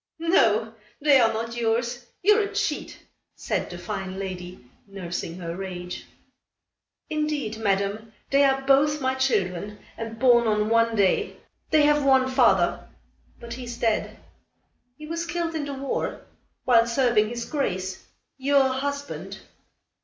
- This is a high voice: Yes, high, 235 Hz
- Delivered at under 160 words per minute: Yes, average, 140 wpm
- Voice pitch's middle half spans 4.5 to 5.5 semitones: Yes, average, 5.1 semitones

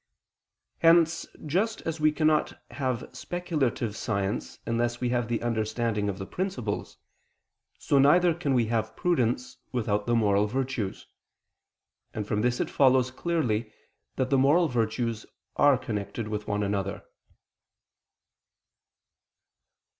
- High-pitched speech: No, low, 120 Hz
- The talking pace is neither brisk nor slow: No, slow, 125 wpm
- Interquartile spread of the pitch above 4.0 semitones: Yes, average, 5.0 semitones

